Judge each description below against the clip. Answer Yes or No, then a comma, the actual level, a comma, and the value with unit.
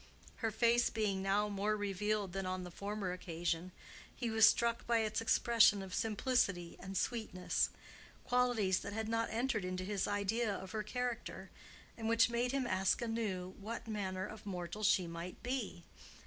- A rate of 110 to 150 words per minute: No, average, 160 wpm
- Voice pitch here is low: No, high, 210 Hz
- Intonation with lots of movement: No, average, 3.4 semitones